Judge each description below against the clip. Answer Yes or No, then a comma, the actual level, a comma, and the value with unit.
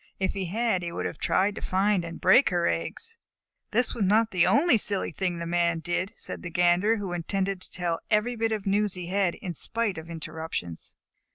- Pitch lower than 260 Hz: Yes, high, 190 Hz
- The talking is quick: Yes, fast, 210 wpm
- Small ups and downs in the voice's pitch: No, average, 3.4 semitones